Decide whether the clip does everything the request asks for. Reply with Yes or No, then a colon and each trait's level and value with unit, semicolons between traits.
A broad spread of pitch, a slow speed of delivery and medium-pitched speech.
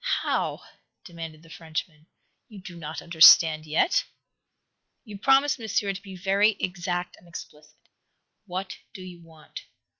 No: average, 3.5 semitones; slow, 130 wpm; medium, 175 Hz